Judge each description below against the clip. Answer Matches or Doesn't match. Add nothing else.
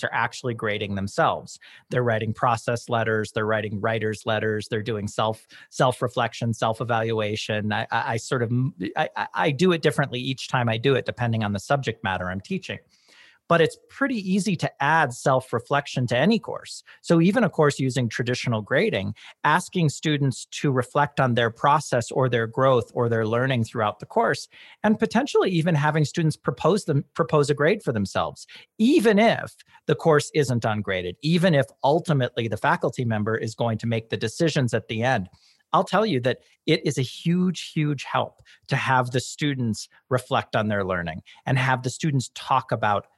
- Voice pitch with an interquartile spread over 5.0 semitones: Matches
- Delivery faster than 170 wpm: Matches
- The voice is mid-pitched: Doesn't match